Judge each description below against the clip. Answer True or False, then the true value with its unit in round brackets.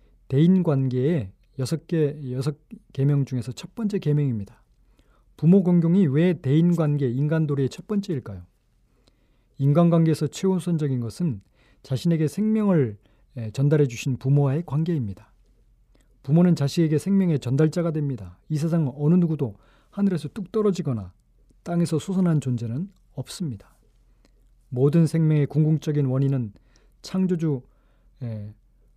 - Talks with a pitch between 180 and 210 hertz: False (145 Hz)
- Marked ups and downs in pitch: False (4.8 semitones)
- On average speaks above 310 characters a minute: False (295 characters per minute)